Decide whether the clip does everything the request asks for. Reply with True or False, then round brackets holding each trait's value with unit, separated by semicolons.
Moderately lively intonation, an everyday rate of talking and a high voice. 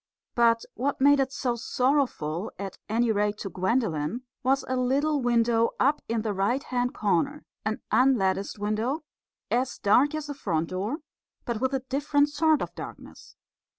True (4.6 semitones; 160 wpm; 245 Hz)